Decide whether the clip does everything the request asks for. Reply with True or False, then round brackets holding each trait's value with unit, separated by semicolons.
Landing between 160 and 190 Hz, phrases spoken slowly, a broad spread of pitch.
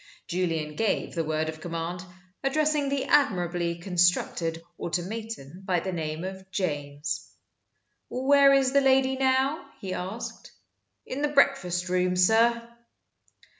True (185 Hz; 125 wpm; 7.7 semitones)